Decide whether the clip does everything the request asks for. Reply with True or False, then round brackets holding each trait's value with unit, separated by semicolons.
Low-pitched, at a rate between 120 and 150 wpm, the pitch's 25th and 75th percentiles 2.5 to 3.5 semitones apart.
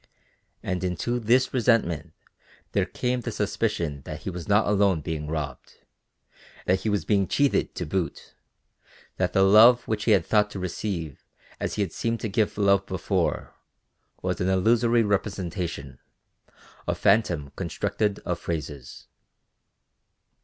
False (100 Hz; 140 wpm; 4.4 semitones)